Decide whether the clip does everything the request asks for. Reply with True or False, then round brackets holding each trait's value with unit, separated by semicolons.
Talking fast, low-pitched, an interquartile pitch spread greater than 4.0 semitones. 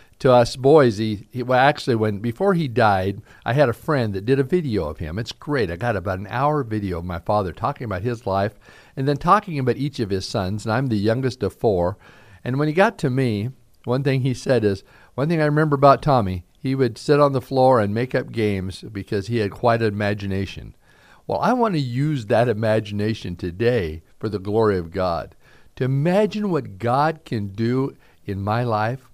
True (215 wpm; 120 Hz; 4.8 semitones)